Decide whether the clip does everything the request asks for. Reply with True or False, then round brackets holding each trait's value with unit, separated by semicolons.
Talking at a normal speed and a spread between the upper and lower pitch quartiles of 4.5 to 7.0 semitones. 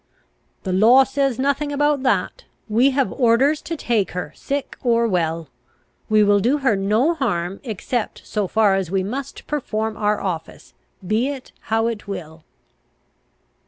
True (155 wpm; 5.5 semitones)